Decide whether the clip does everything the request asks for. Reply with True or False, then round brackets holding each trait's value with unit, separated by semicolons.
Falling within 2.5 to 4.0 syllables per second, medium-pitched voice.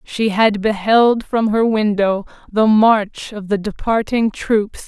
False (3.5 syllables/s; 215 Hz)